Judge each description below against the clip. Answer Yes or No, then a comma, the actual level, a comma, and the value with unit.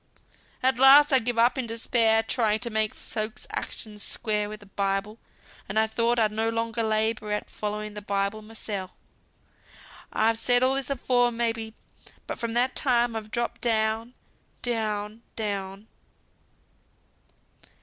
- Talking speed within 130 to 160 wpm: Yes, average, 150 wpm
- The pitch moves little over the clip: Yes, narrow, 2.0 semitones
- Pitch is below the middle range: No, high, 225 Hz